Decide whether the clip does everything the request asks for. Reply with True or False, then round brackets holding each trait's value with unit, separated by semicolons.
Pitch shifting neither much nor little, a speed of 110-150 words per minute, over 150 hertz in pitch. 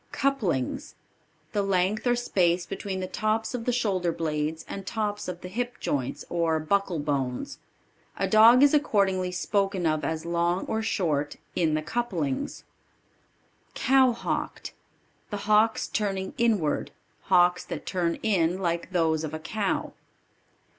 True (4.7 semitones; 140 wpm; 185 Hz)